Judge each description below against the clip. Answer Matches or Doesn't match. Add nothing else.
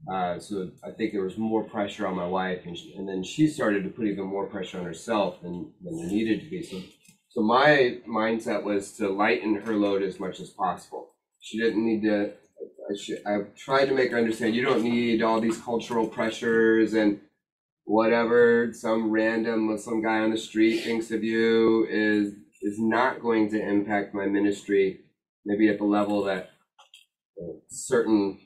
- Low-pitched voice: Matches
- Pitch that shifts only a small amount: Matches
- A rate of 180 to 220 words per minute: Matches